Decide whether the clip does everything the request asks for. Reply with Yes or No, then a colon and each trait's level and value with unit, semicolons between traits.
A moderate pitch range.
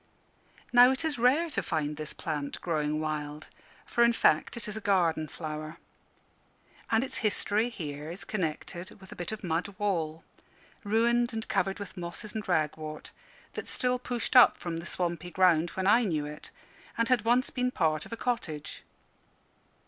No: wide, 6.7 semitones